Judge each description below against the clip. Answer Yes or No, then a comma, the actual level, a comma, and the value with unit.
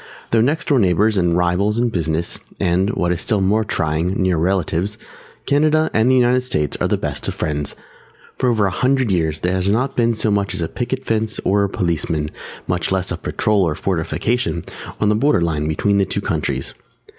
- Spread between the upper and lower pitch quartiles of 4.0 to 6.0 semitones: Yes, average, 4.9 semitones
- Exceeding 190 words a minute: Yes, fast, 205 wpm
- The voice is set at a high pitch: No, low, 100 Hz